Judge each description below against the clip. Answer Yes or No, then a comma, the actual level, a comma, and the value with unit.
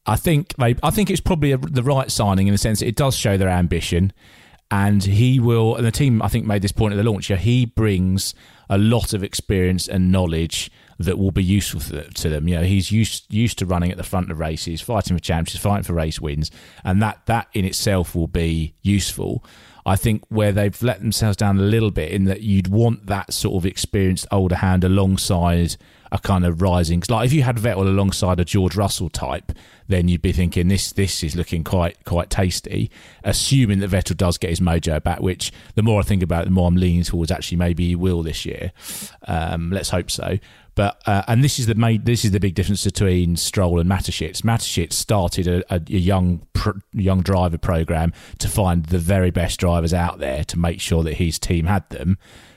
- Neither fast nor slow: No, fast, 220 wpm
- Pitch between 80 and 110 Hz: Yes, very low, 95 Hz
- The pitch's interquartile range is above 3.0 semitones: Yes, average, 3.4 semitones